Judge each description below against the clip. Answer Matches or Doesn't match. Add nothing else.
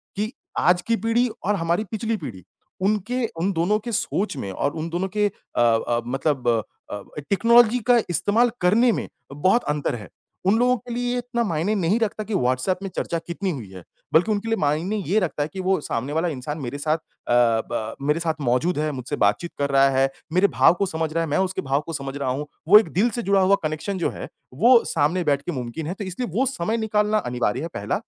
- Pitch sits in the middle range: Matches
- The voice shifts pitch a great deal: Matches